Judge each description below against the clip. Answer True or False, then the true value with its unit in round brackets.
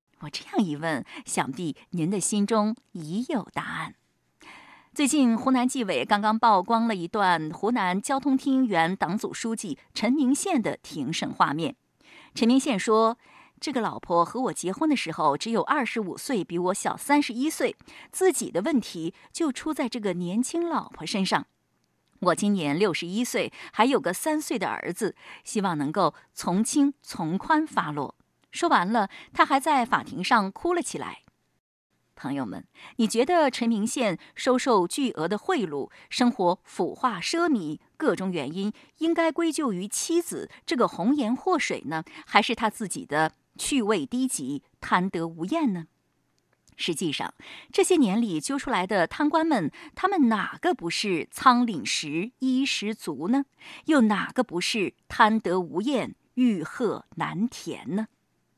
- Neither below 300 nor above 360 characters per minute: False (230 characters per minute)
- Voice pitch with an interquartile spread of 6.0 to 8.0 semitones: True (6.3 semitones)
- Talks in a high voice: True (235 Hz)